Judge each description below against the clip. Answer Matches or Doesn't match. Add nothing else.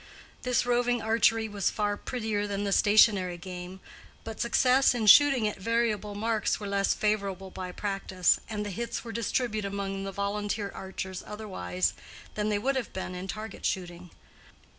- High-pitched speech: Matches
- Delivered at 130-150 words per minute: Doesn't match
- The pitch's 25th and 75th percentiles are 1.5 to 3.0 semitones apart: Matches